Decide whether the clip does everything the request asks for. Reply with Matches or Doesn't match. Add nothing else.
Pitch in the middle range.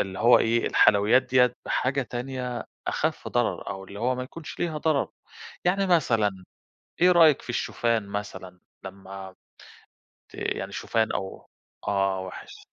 Doesn't match